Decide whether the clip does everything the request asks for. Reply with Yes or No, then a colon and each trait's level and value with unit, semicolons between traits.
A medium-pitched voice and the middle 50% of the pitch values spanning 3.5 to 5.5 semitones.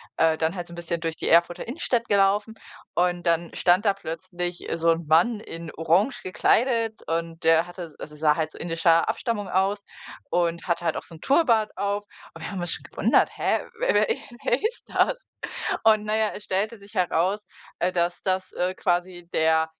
Yes: medium, 180 Hz; average, 3.9 semitones